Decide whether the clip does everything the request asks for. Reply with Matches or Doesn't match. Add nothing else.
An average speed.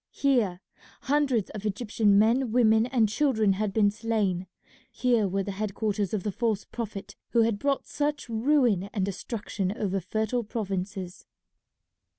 Matches